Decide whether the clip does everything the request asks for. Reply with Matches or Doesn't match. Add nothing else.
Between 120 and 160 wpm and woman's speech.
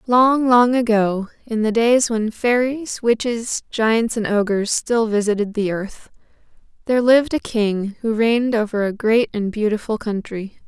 Matches